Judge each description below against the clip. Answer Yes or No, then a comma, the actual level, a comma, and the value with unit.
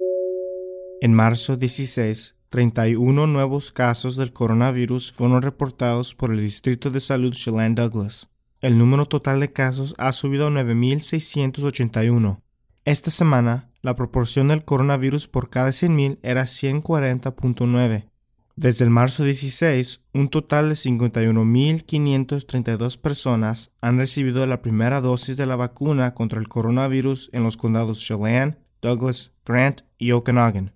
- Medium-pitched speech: No, low, 125 Hz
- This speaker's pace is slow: Yes, slow, 125 wpm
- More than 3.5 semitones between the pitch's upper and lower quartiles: No, average, 2.8 semitones